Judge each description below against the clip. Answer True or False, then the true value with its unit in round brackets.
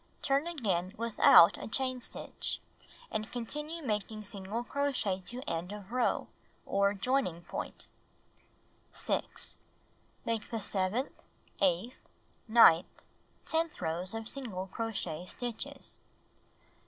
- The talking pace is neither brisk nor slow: False (105 wpm)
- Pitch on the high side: True (220 Hz)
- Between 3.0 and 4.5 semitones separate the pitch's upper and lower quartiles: False (5.0 semitones)